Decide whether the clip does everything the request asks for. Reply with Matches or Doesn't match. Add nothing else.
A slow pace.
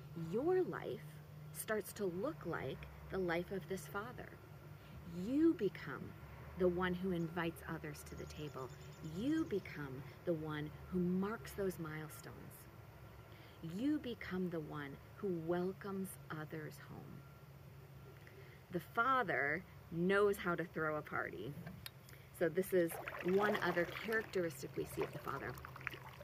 Matches